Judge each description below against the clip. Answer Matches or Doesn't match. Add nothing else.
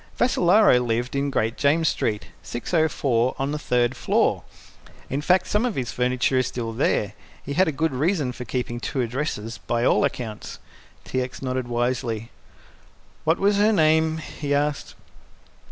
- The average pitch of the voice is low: Matches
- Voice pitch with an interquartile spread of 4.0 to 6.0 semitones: Matches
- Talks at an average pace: Matches